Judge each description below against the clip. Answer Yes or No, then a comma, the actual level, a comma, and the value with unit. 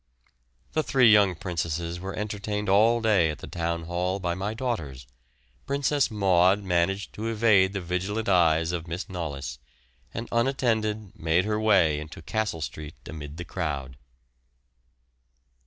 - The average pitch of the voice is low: Yes, very low, 95 Hz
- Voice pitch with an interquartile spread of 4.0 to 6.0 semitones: Yes, average, 4.5 semitones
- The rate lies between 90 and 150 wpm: Yes, average, 140 wpm